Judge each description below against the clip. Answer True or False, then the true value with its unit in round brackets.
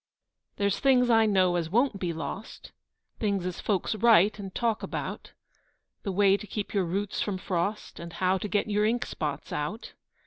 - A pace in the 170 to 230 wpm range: True (180 wpm)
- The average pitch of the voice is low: False (200 Hz)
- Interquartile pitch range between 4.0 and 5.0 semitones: False (2.8 semitones)